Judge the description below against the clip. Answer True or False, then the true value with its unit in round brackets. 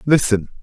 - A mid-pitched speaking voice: False (125 Hz)